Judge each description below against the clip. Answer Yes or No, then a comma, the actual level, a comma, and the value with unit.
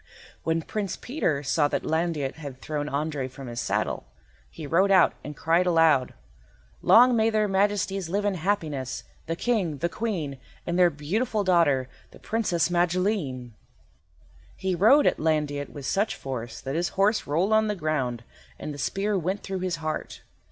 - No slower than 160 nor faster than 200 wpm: Yes, average, 165 wpm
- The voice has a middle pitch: Yes, medium, 165 Hz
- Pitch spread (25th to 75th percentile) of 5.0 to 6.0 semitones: Yes, wide, 5.4 semitones